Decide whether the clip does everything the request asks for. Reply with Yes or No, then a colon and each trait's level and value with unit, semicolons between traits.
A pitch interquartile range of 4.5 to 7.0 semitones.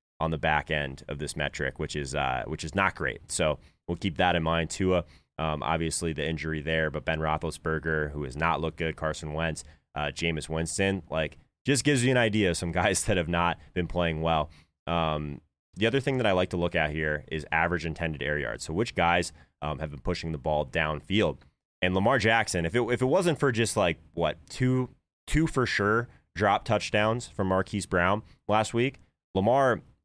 No: average, 4.0 semitones